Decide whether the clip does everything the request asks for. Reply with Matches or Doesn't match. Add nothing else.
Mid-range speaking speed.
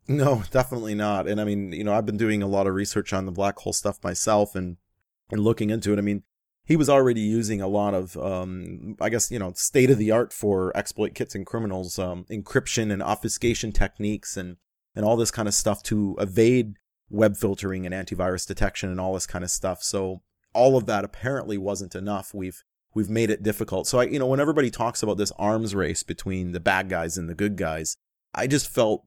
Doesn't match